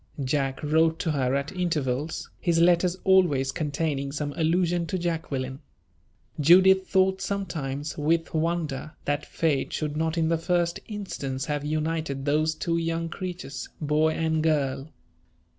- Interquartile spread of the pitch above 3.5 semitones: No, average, 2.9 semitones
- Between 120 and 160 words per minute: Yes, average, 140 wpm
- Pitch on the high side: No, medium, 160 Hz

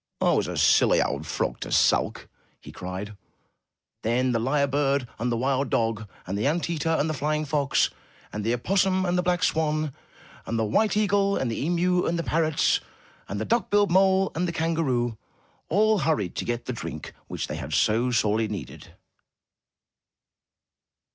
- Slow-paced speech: No, average, 180 wpm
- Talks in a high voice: No, medium, 145 Hz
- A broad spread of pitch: Yes, wide, 7.2 semitones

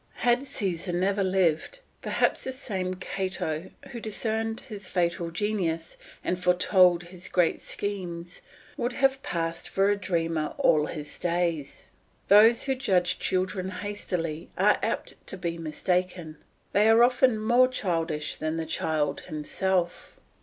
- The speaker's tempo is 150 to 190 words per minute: No, slow, 135 wpm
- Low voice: No, medium, 185 Hz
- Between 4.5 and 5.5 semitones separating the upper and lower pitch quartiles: No, average, 3.7 semitones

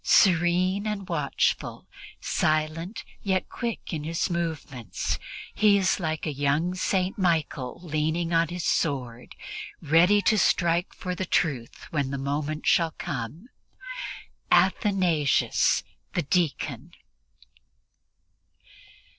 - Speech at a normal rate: No, slow, 105 wpm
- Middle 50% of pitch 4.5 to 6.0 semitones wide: No, average, 3.5 semitones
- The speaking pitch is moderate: Yes, medium, 165 Hz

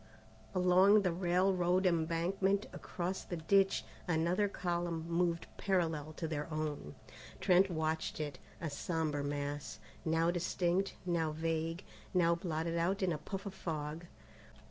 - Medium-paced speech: No, slow, 130 wpm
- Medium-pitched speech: Yes, medium, 170 Hz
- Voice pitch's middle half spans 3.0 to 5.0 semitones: No, narrow, 2.4 semitones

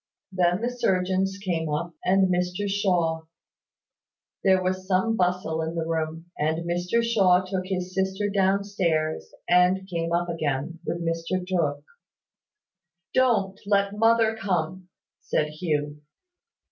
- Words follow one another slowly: Yes, slow, 130 wpm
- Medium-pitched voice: Yes, medium, 180 Hz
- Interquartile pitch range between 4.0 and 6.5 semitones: No, average, 2.7 semitones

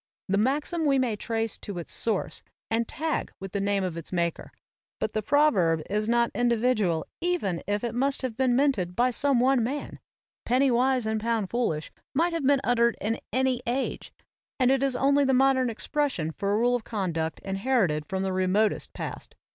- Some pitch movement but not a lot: Yes, average, 4.9 semitones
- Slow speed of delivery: No, average, 190 wpm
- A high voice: Yes, high, 235 Hz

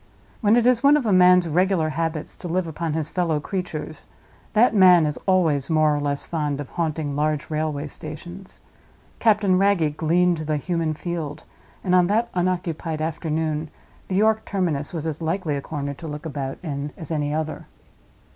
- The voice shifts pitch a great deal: No, average, 3.3 semitones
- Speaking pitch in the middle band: Yes, medium, 160 Hz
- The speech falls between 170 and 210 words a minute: Yes, average, 175 wpm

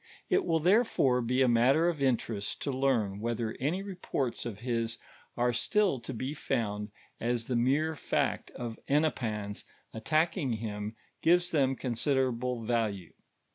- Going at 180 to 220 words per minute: No, average, 140 wpm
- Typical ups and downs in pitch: Yes, average, 4.2 semitones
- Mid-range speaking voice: No, low, 125 Hz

